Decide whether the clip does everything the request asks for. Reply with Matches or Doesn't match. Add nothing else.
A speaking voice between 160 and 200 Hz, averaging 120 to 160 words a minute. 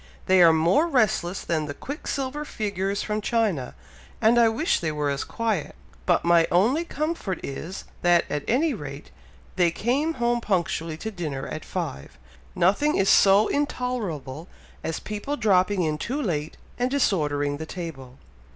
Matches